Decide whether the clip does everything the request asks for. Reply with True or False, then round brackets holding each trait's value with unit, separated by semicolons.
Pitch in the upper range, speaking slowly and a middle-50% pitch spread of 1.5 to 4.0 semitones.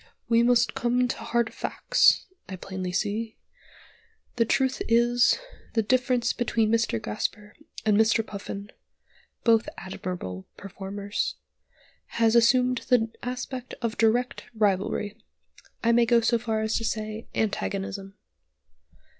True (225 Hz; 120 wpm; 2.6 semitones)